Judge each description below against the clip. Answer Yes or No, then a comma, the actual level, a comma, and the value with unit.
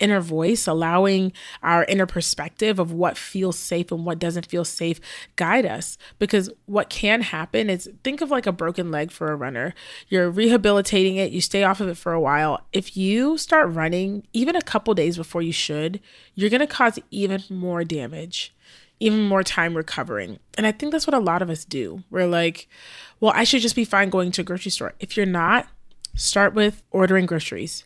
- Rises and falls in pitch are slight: No, average, 3.7 semitones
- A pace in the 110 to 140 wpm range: No, average, 200 wpm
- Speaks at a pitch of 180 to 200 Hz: Yes, high, 190 Hz